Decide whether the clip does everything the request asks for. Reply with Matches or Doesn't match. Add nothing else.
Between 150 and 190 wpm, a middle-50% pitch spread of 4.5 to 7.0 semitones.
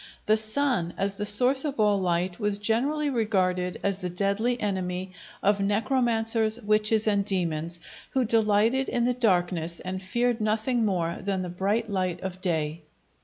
Doesn't match